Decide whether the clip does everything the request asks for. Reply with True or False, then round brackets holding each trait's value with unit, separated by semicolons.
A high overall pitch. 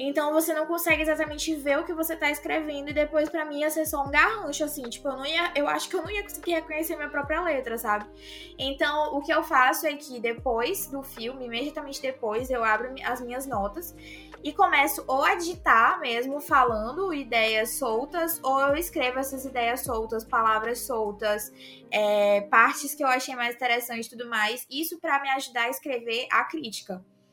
True (275 Hz)